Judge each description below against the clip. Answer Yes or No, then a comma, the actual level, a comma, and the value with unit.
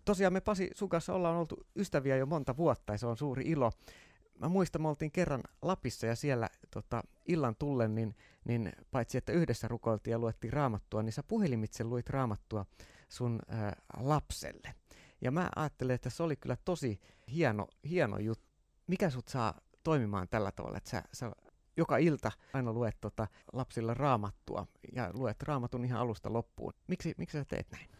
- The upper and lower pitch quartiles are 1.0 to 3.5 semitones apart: No, wide, 5.6 semitones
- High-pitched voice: No, low, 125 Hz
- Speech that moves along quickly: Yes, fast, 175 wpm